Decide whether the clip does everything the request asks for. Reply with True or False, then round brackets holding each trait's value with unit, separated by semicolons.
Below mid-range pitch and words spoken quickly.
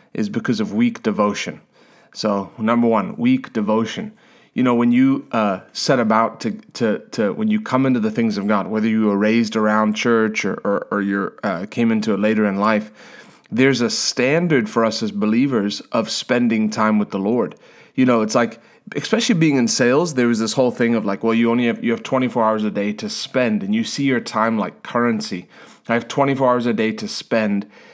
True (120 Hz; 215 wpm)